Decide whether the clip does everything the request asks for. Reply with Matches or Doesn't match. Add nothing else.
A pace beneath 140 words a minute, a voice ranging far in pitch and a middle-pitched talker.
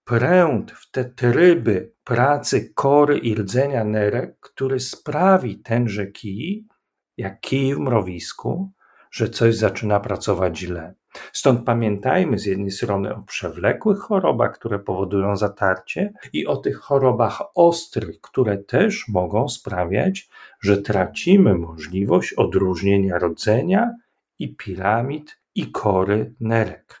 Doesn't match